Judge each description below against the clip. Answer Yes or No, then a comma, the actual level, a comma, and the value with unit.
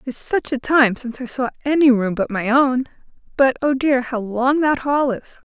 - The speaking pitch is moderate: No, very high, 260 Hz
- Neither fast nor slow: No, fast, 230 wpm